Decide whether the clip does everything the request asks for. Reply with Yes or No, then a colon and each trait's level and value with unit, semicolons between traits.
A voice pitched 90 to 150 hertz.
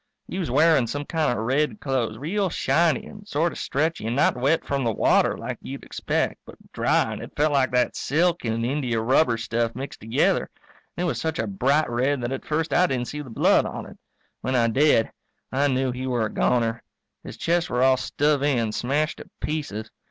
Yes: low, 135 Hz